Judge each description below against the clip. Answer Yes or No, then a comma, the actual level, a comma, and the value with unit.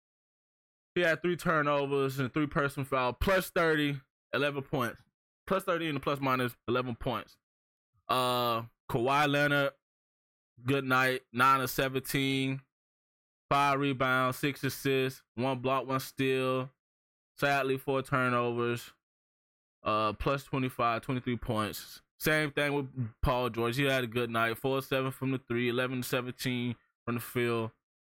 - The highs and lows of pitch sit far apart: No, narrow, 2.4 semitones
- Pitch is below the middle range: Yes, low, 130 Hz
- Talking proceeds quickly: No, average, 140 wpm